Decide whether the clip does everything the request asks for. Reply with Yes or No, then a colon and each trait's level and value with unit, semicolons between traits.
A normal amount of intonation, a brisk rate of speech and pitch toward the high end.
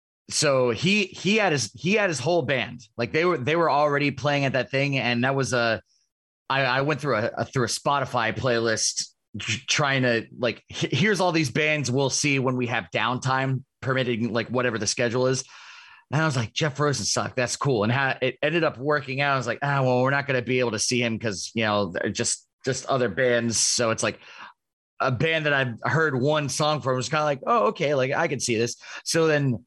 No: average, 3.6 semitones; fast, 235 wpm; low, 130 Hz